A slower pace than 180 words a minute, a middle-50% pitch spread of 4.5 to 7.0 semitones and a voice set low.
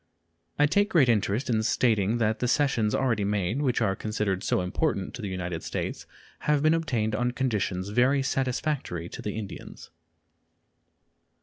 Yes: average, 160 wpm; average, 5.0 semitones; low, 110 Hz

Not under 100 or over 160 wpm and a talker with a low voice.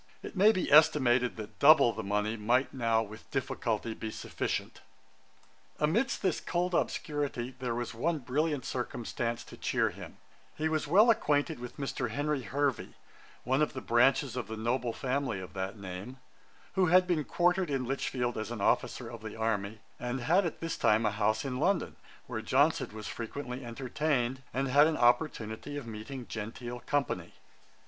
No: average, 170 wpm; low, 125 Hz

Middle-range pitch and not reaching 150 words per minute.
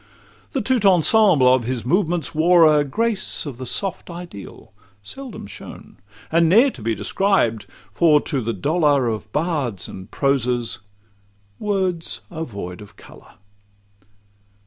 Yes: medium, 150 Hz; slow, 135 wpm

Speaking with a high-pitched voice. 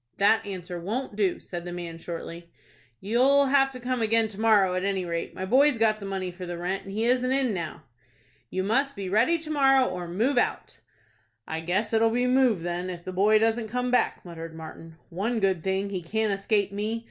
Yes: high, 200 Hz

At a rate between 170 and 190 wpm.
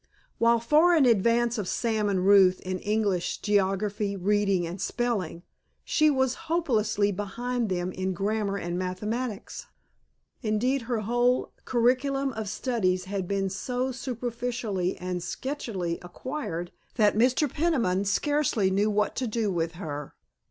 No: slow, 135 wpm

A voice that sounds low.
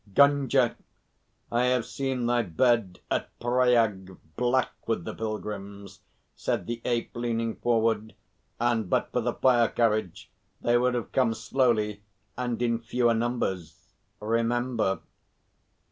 Yes: low, 115 Hz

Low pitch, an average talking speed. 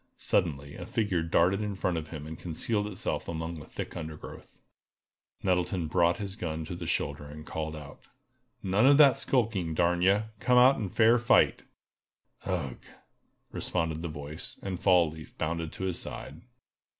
Yes: very low, 85 Hz; average, 165 wpm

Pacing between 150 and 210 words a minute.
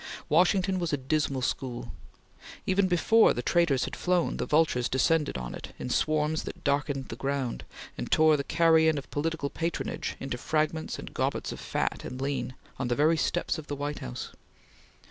Yes: average, 180 wpm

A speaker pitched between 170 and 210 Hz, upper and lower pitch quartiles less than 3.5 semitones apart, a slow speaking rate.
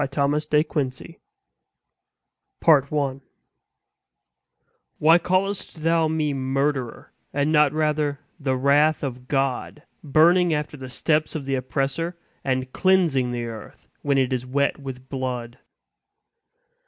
No: medium, 140 Hz; average, 2.8 semitones; slow, 120 wpm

